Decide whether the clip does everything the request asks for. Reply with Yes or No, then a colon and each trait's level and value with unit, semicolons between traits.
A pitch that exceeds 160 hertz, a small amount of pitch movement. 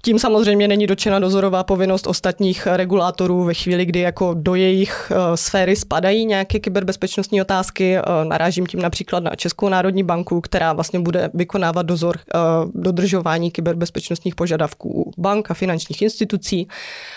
Yes: medium, 185 Hz; narrow, 2.2 semitones